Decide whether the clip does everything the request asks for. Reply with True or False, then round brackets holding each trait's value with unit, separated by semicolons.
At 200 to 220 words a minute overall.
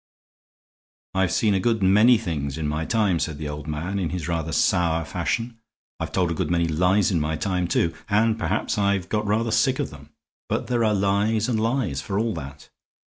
True (205 wpm)